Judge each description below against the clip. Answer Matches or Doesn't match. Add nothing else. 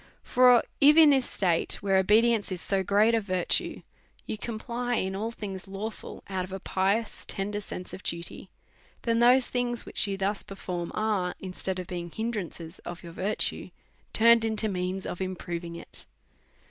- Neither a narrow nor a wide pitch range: Matches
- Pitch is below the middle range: Doesn't match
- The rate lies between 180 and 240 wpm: Doesn't match